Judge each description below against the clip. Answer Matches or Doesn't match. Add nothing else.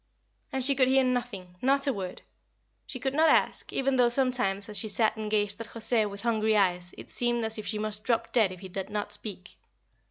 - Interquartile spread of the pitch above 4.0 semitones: Doesn't match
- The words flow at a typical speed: Doesn't match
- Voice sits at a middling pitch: Doesn't match